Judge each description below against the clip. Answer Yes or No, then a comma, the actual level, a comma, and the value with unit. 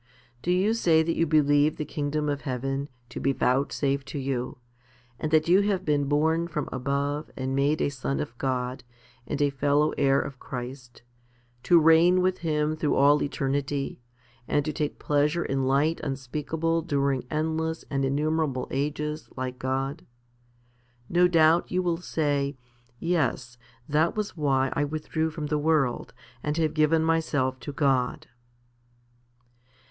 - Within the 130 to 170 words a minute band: Yes, average, 150 wpm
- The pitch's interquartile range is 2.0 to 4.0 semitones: Yes, average, 2.7 semitones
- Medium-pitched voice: Yes, medium, 145 Hz